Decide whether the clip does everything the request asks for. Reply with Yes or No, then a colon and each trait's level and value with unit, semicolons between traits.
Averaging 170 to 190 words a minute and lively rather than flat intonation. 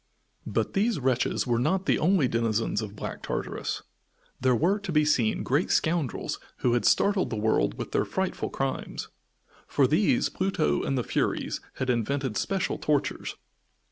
No: average, 160 wpm; wide, 7.6 semitones